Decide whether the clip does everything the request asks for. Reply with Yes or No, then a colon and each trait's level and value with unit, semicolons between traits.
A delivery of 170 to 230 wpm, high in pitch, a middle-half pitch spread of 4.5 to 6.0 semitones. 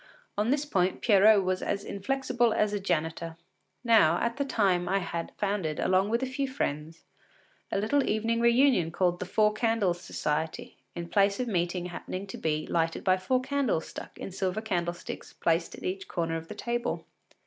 Yes: average, 180 wpm; high, 195 Hz; average, 5.0 semitones